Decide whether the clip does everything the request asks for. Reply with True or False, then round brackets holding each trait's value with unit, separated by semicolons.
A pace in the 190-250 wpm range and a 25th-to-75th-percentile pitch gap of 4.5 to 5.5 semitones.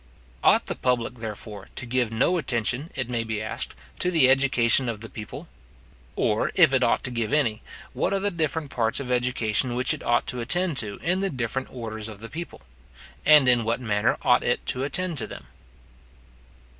False (195 wpm; 3.6 semitones)